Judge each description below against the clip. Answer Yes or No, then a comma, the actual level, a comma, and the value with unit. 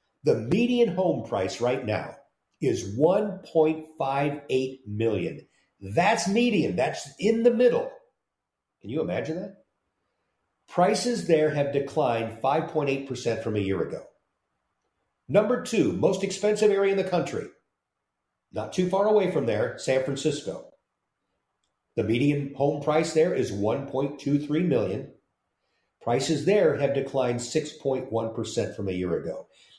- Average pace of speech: No, slow, 125 wpm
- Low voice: No, medium, 145 Hz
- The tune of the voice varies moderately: No, wide, 6.6 semitones